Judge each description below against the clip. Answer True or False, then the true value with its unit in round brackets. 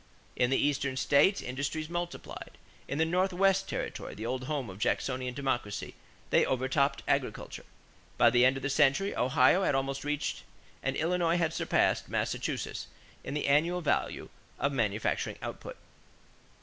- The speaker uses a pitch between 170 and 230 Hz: False (140 Hz)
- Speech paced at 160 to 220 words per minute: False (150 wpm)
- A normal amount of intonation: True (4.1 semitones)